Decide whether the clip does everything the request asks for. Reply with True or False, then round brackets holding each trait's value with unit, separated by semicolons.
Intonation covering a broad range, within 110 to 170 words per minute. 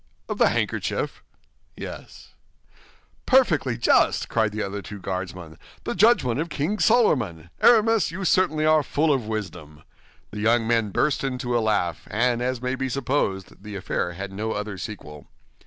True (6.7 semitones; 155 wpm)